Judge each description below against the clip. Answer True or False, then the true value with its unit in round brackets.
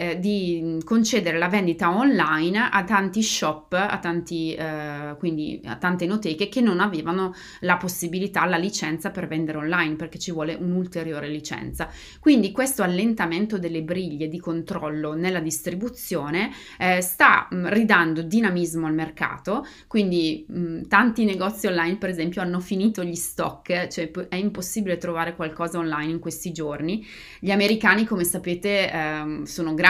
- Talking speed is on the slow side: False (145 wpm)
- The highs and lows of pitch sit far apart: False (3.2 semitones)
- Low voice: False (175 Hz)